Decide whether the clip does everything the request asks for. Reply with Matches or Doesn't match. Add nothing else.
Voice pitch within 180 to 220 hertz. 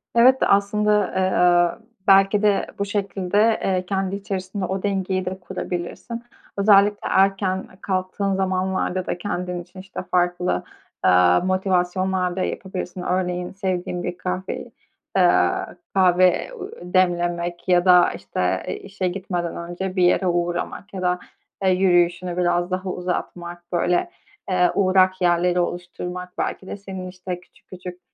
Matches